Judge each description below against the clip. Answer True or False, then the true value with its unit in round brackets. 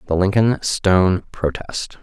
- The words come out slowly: True (120 wpm)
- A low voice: True (95 Hz)